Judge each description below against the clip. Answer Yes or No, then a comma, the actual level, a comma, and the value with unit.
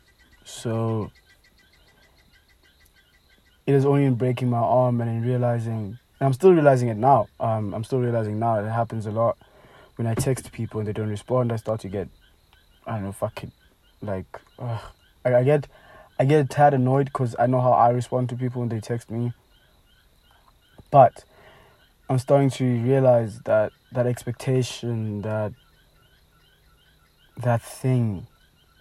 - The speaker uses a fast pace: No, average, 145 wpm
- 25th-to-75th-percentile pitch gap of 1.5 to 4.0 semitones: Yes, average, 3.0 semitones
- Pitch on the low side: Yes, low, 120 Hz